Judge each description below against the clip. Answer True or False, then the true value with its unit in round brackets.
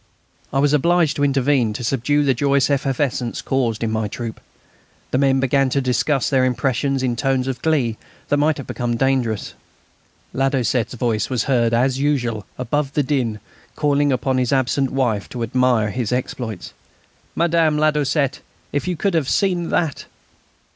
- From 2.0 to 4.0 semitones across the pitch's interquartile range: True (2.9 semitones)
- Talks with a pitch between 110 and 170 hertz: True (135 Hz)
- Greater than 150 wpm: True (160 wpm)